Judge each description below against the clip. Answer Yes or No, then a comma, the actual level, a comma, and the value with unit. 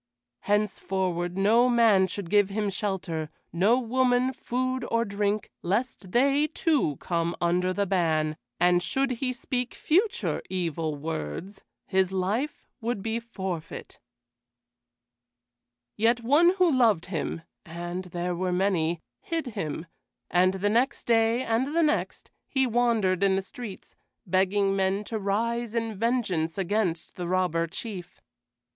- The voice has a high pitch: Yes, high, 200 Hz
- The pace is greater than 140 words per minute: No, slow, 135 wpm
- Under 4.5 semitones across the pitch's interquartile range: No, average, 4.9 semitones